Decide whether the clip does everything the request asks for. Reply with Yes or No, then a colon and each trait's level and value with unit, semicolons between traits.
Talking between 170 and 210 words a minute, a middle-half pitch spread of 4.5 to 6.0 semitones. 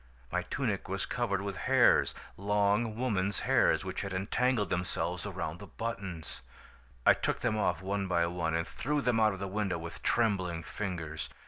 No: average, 175 wpm; average, 3.3 semitones